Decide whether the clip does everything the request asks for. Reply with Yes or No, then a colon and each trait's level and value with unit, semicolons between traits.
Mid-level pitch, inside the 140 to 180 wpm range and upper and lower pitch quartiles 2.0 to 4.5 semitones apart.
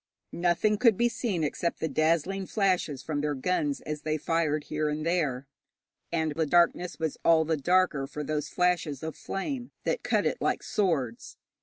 Yes: medium, 160 Hz; average, 175 wpm; average, 3.3 semitones